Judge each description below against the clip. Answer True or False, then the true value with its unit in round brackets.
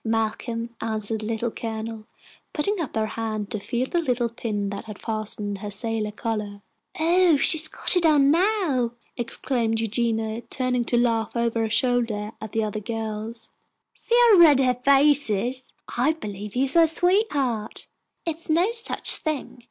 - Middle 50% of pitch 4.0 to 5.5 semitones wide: True (4.7 semitones)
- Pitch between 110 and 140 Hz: False (235 Hz)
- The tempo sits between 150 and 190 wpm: True (170 wpm)